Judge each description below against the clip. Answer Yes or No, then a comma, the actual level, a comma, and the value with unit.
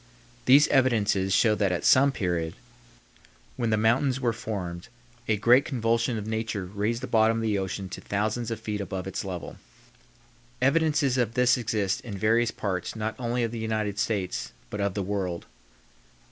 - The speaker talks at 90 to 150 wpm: No, average, 175 wpm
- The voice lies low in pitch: Yes, low, 110 Hz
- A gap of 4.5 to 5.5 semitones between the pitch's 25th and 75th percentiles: No, average, 3.0 semitones